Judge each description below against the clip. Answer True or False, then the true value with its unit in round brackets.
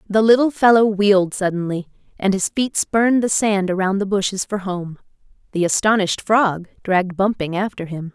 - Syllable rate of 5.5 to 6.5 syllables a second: False (5.3 syllables/s)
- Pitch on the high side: True (200 Hz)